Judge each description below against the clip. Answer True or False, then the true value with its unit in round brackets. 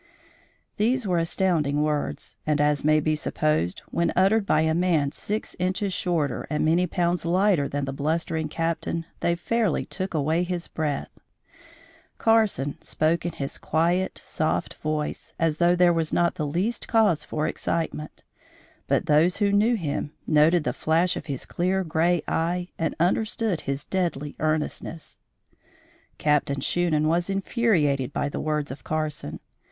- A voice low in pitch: False (165 Hz)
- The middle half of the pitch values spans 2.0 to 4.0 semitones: True (3.0 semitones)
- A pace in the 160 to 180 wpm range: False (150 wpm)